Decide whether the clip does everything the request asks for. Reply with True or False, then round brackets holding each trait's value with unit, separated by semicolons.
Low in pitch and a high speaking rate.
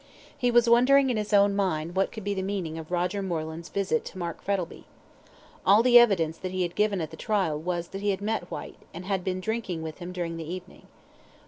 False (185 Hz; 230 wpm)